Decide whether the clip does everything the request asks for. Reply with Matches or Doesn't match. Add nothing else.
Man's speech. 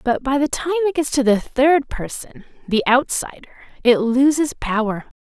Doesn't match